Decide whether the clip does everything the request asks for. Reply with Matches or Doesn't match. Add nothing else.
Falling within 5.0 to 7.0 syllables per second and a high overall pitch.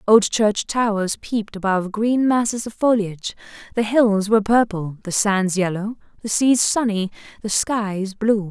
Doesn't match